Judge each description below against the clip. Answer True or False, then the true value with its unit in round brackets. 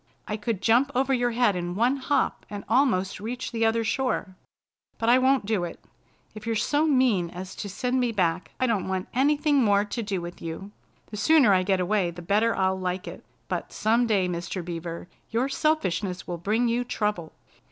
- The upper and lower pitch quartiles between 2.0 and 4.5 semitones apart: False (4.9 semitones)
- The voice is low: False (210 Hz)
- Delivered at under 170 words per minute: False (200 wpm)